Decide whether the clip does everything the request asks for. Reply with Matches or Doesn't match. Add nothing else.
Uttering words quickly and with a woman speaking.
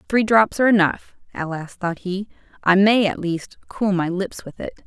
Matches